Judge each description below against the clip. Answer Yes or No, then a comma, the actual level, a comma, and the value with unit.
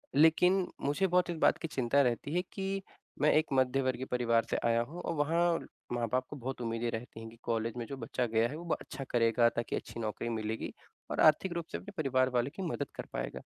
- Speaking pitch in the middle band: No, low, 130 Hz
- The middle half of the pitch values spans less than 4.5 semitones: No, average, 5.1 semitones